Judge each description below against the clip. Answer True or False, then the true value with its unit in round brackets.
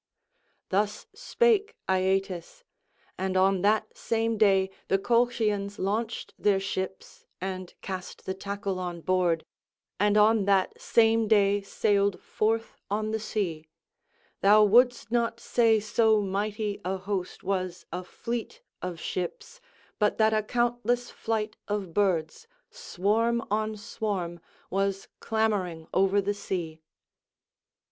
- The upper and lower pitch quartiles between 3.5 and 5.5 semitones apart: False (2.7 semitones)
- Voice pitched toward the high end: True (205 Hz)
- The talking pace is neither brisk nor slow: False (120 wpm)